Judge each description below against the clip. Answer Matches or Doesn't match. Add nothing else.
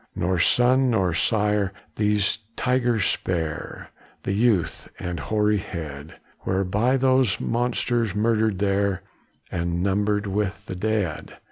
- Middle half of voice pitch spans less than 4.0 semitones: Matches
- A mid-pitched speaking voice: Doesn't match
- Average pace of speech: Doesn't match